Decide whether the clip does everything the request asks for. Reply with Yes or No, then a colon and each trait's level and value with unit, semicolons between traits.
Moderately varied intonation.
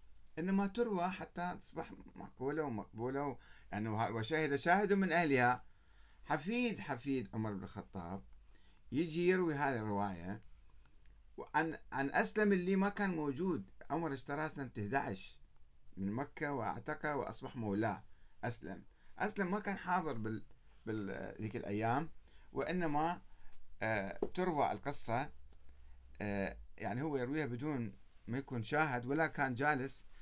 No: wide, 7.8 semitones